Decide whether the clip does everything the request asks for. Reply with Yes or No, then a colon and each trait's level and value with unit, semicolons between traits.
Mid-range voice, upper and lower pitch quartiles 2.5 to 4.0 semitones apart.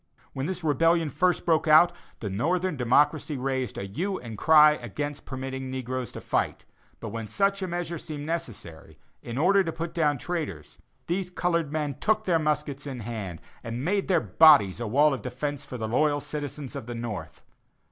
No: medium, 145 Hz; average, 5.1 semitones